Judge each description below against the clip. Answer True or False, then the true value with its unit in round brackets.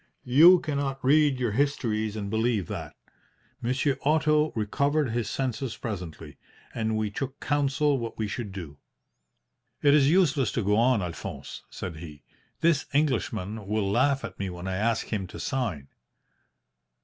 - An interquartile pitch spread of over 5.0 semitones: True (5.5 semitones)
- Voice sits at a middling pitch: False (120 Hz)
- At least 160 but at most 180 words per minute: False (150 wpm)